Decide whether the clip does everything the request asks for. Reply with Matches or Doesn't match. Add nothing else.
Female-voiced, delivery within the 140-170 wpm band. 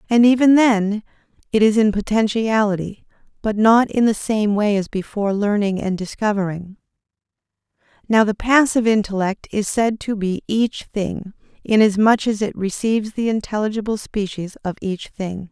Matches